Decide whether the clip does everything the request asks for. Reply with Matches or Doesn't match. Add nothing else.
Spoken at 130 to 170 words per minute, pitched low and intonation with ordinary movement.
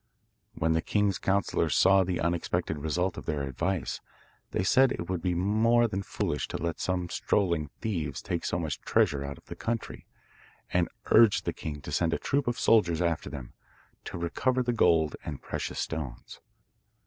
Doesn't match